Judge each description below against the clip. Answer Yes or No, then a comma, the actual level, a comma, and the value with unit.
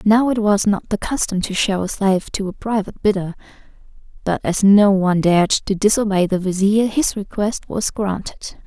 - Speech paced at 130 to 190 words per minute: Yes, average, 185 wpm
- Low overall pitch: No, high, 200 Hz